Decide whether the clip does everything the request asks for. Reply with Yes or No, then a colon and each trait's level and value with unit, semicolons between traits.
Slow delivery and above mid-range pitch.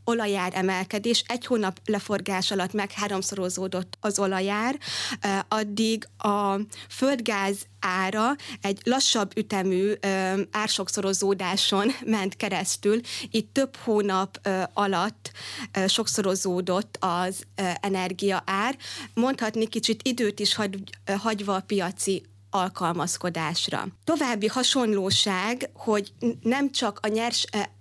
Yes: slow, 90 wpm; high, 205 Hz